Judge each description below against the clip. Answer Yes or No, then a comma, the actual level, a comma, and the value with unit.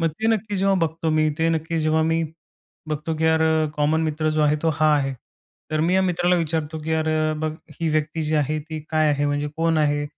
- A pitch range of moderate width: No, narrow, 1.2 semitones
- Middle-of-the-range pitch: Yes, medium, 155 Hz